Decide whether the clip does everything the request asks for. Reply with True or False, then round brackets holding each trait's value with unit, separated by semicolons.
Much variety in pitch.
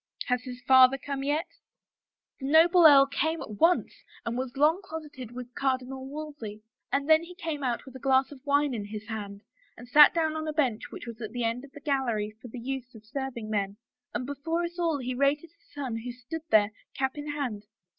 False (3.7 semitones)